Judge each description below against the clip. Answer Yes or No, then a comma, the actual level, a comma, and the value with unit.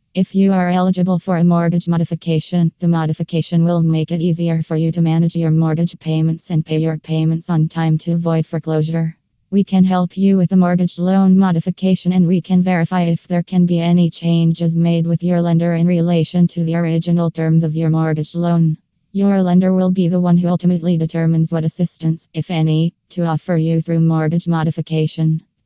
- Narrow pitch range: Yes, narrow, 1.5 semitones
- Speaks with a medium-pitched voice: Yes, medium, 170 Hz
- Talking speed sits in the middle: Yes, average, 190 wpm